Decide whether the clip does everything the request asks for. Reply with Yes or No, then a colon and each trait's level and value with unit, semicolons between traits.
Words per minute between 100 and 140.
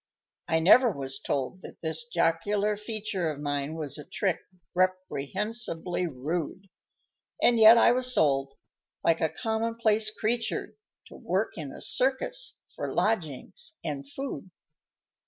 Yes: slow, 135 wpm